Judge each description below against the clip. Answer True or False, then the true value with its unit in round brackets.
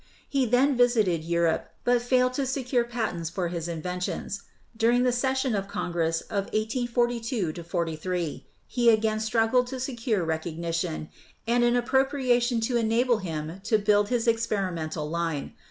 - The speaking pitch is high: True (220 Hz)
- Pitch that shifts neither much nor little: False (6.2 semitones)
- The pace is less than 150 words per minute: True (140 wpm)